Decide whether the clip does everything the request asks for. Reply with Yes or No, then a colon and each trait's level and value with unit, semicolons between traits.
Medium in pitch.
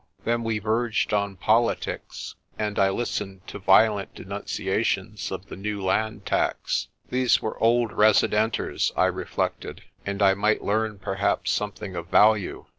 No: low, 105 Hz